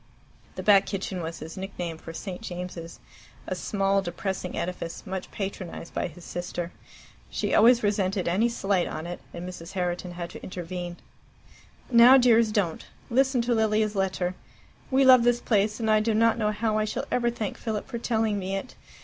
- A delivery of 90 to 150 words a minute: No, average, 180 wpm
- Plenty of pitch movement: No, average, 3.8 semitones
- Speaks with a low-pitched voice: No, high, 195 Hz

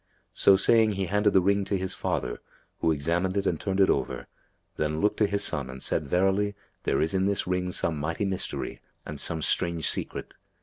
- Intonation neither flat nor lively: Yes, average, 3.4 semitones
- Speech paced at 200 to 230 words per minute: Yes, fast, 205 wpm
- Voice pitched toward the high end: No, very low, 95 Hz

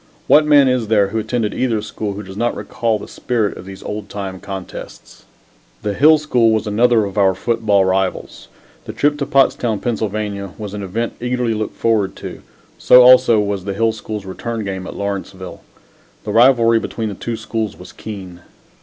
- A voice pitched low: Yes, low, 110 Hz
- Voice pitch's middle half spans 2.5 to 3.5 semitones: Yes, average, 3.0 semitones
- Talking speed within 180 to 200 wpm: Yes, average, 185 wpm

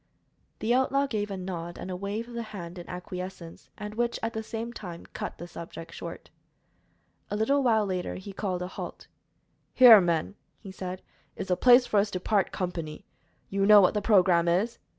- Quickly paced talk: No, average, 190 wpm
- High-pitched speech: Yes, high, 195 Hz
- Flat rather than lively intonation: No, average, 3.5 semitones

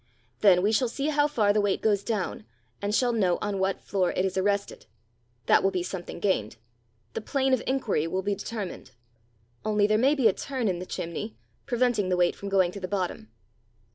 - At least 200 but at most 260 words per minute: Yes, fast, 205 wpm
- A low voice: No, high, 205 Hz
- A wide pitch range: No, average, 3.5 semitones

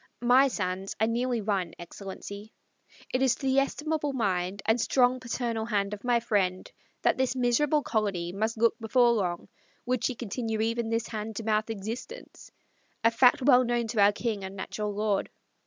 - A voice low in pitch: No, high, 225 Hz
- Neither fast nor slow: Yes, average, 175 wpm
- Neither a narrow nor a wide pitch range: Yes, average, 3.4 semitones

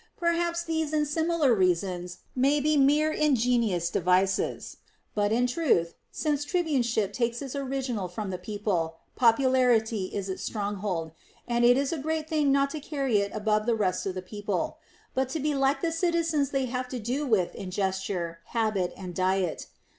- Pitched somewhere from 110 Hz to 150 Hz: No, high, 240 Hz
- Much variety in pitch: Yes, wide, 6.7 semitones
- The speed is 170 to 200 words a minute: Yes, average, 175 wpm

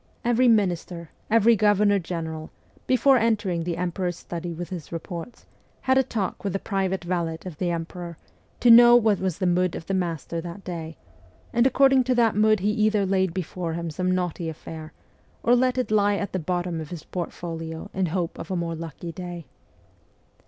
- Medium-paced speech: Yes, average, 190 wpm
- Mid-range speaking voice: Yes, medium, 180 Hz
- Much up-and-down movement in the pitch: No, average, 3.8 semitones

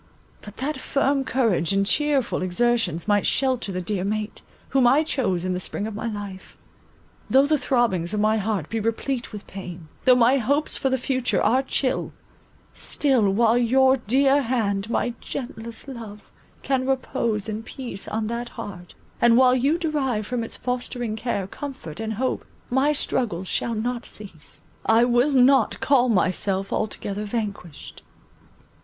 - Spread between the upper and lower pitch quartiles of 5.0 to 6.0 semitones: No, average, 4.2 semitones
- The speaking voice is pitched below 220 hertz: No, high, 235 Hz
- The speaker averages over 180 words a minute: No, average, 160 wpm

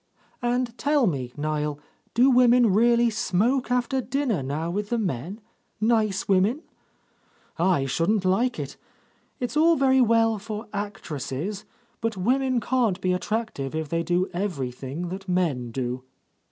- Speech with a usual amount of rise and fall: No, wide, 6.3 semitones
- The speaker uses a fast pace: No, average, 140 wpm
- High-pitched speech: Yes, high, 205 Hz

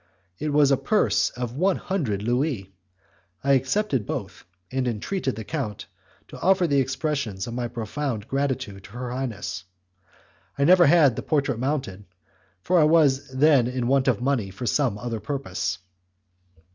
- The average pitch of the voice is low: Yes, low, 130 Hz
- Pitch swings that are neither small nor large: Yes, average, 4.0 semitones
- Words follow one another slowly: No, average, 160 wpm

